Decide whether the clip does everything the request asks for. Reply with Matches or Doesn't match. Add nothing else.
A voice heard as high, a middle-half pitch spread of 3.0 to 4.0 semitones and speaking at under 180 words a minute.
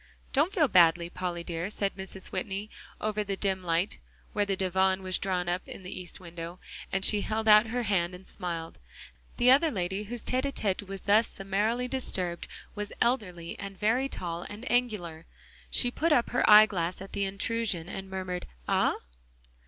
Doesn't match